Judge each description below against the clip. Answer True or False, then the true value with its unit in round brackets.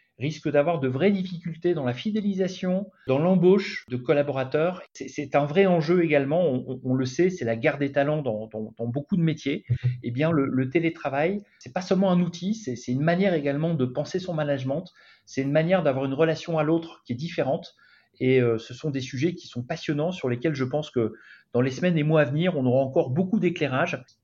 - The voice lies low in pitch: False (150 Hz)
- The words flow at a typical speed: False (225 wpm)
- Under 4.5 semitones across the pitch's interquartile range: False (4.9 semitones)